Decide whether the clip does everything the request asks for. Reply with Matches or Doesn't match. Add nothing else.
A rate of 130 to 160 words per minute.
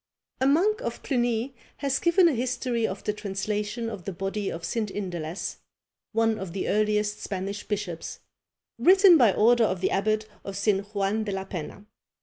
Doesn't match